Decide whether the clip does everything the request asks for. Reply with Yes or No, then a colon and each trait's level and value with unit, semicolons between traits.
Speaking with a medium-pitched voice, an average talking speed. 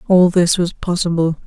Yes: medium, 175 Hz; average, 165 wpm